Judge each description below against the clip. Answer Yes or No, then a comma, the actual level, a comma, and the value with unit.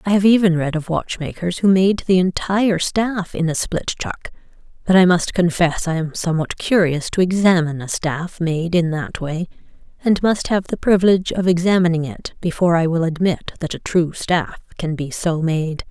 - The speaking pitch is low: No, medium, 175 Hz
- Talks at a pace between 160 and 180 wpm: No, average, 190 wpm